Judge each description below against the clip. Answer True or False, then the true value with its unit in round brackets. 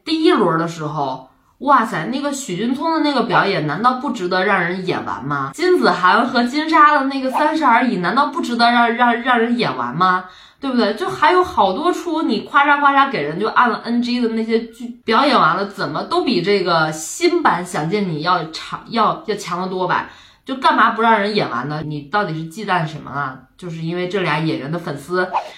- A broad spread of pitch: True (7.6 semitones)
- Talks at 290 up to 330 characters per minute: True (305 characters per minute)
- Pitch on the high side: True (220 Hz)